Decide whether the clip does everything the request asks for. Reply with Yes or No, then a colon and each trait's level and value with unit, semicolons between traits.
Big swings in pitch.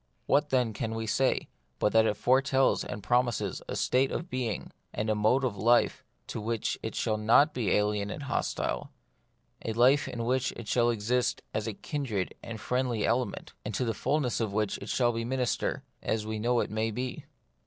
No: average, 2.9 semitones